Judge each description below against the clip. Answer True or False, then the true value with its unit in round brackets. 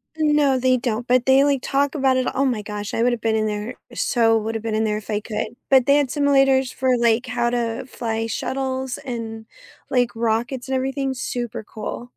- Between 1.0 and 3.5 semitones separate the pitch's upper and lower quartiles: True (2.9 semitones)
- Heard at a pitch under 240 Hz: False (245 Hz)